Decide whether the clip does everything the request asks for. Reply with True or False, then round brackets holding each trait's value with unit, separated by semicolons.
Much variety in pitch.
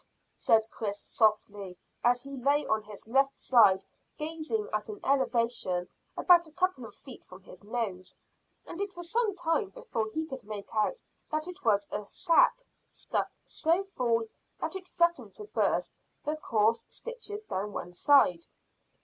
True (8.2 semitones)